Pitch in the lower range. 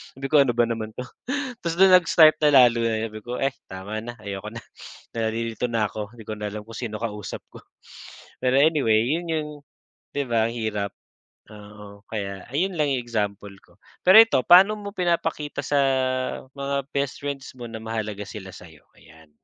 Yes: low, 115 Hz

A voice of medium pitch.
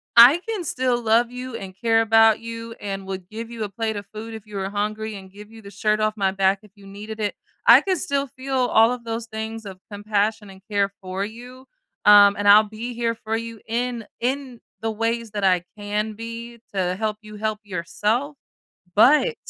No: high, 220 Hz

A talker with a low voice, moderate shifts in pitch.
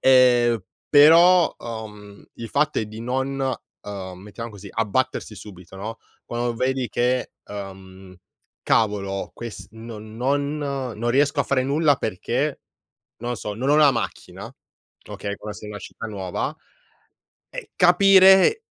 Yes: low, 120 Hz; average, 4.8 semitones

